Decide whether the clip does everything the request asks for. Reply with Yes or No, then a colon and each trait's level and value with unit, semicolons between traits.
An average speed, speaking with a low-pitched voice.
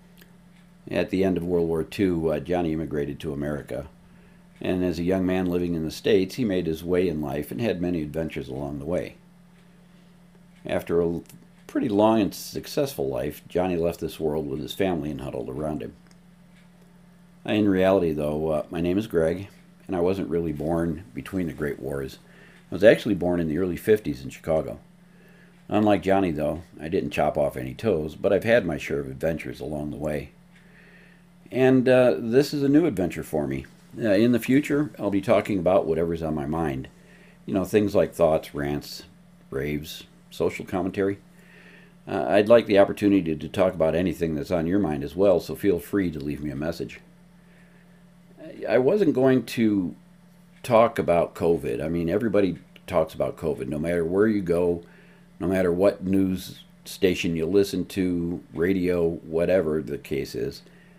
Yes: average, 180 wpm; very low, 95 Hz